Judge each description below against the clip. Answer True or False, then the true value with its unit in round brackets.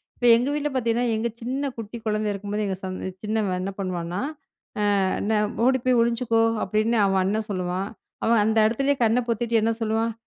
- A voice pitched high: True (220 Hz)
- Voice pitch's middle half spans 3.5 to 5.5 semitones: False (2.7 semitones)